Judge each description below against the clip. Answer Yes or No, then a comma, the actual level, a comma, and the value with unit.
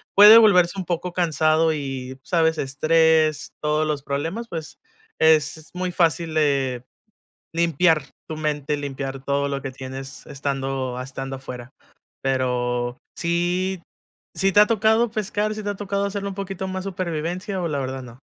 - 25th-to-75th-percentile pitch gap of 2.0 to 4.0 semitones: No, average, 5.3 semitones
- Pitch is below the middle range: No, medium, 155 Hz